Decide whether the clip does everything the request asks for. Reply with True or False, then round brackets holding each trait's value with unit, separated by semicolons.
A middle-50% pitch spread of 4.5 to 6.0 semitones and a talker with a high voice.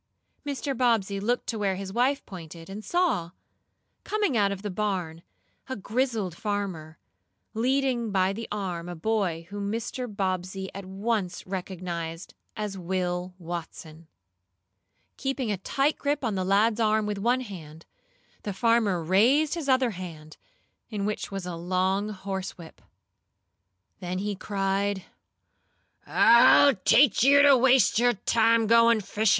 False (4.1 semitones; 200 Hz)